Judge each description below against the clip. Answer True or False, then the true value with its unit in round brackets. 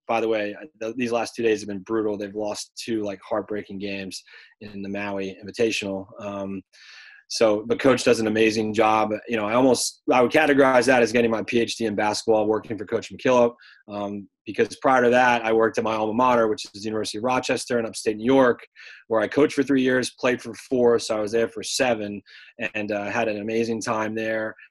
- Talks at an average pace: False (215 wpm)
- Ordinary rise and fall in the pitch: False (2.2 semitones)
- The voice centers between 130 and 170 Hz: False (110 Hz)